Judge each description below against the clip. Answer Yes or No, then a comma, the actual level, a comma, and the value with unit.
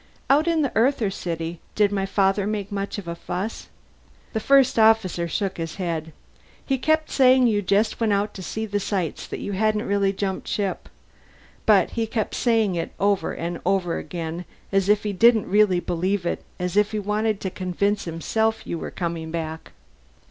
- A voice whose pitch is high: Yes, high, 200 Hz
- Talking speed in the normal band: Yes, average, 185 wpm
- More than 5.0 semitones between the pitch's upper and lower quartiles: No, average, 3.4 semitones